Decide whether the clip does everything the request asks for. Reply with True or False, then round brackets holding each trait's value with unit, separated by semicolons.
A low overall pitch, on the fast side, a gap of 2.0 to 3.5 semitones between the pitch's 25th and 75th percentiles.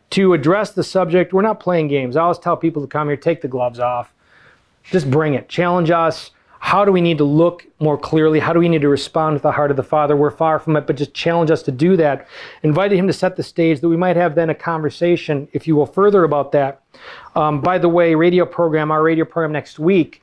False (160 Hz; 250 wpm; 2.8 semitones)